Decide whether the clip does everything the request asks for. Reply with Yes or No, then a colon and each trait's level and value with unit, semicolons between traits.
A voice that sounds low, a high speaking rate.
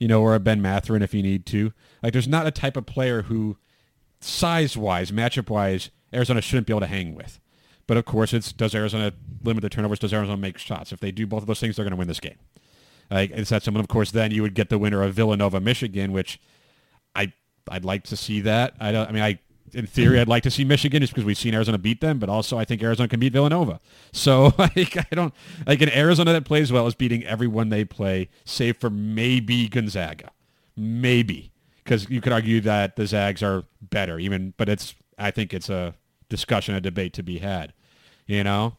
Yes: low, 110 Hz; fast, 230 wpm